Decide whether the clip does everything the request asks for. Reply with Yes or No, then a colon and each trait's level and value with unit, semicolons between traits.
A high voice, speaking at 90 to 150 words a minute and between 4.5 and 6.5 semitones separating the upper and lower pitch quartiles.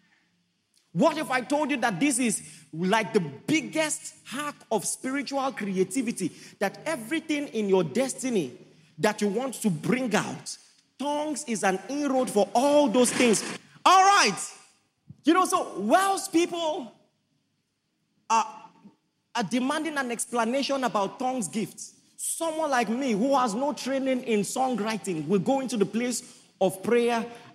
Yes: high, 245 Hz; average, 140 wpm; average, 5.1 semitones